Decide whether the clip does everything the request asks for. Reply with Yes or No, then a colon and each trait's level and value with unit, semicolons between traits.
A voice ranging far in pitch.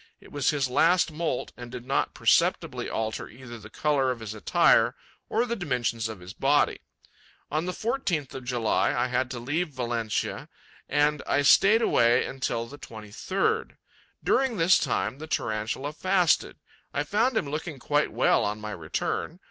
Yes: wide, 5.8 semitones